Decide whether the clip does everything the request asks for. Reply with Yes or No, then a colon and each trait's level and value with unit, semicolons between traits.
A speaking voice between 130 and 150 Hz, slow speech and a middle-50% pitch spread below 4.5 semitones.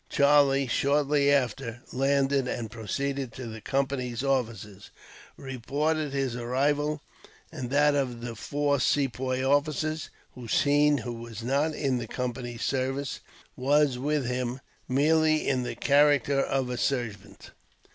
Yes: low, 135 Hz; slow, 125 wpm; average, 2.7 semitones